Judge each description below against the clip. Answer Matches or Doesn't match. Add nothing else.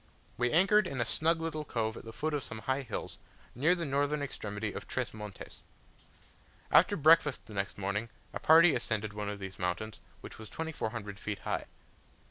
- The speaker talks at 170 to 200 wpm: Matches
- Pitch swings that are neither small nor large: Doesn't match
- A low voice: Matches